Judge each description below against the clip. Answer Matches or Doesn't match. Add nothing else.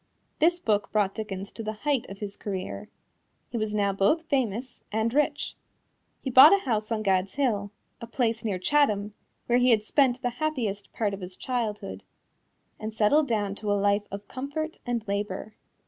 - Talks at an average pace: Matches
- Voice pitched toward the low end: Doesn't match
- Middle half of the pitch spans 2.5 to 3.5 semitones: Doesn't match